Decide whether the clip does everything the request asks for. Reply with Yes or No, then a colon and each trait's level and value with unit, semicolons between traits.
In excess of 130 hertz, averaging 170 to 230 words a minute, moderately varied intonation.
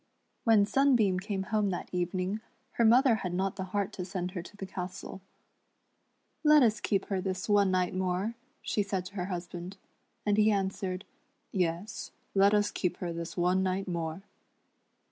No: high, 190 Hz; average, 175 wpm; narrow, 2.2 semitones